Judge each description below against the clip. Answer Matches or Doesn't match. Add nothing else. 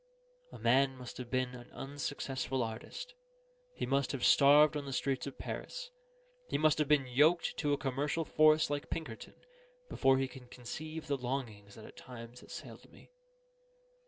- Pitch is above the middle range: Doesn't match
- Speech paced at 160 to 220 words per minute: Matches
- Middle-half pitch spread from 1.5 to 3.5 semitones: Matches